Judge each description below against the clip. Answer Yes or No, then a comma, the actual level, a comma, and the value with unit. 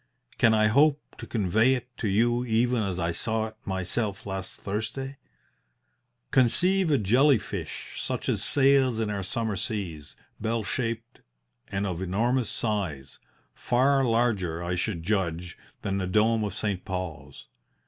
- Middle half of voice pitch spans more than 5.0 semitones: No, average, 4.4 semitones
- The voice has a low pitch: Yes, low, 110 Hz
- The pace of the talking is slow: No, average, 150 wpm